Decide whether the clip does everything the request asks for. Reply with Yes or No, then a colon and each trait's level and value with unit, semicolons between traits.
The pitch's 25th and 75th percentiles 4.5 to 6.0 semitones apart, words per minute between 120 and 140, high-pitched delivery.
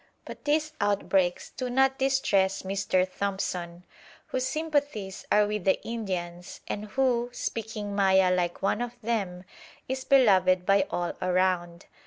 Yes: average, 4.8 semitones; slow, 135 wpm; high, 200 Hz